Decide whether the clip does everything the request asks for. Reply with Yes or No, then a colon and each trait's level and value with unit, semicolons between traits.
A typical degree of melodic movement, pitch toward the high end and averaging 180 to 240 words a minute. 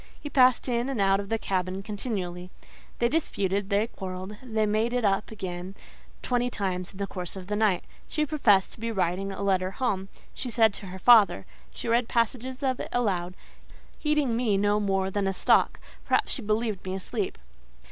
Yes: average, 3.8 semitones; high, 205 Hz; average, 185 wpm